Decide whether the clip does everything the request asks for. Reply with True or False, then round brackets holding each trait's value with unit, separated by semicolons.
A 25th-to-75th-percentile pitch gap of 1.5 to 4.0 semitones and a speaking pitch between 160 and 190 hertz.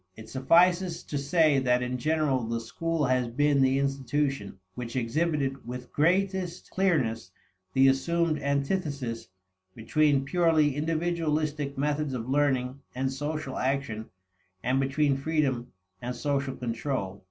False (3.4 semitones; 140 Hz)